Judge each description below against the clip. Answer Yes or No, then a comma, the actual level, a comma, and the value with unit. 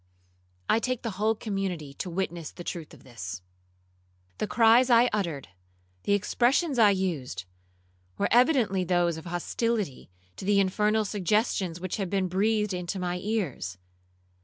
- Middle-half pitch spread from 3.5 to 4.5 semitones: Yes, average, 4.0 semitones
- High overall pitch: Yes, high, 195 Hz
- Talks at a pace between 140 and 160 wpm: Yes, average, 145 wpm